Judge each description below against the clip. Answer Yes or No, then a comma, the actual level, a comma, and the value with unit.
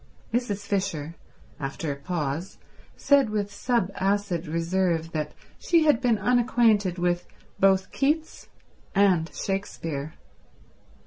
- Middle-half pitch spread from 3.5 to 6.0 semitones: Yes, average, 4.7 semitones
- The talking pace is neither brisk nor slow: No, slow, 110 wpm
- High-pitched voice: Yes, high, 195 Hz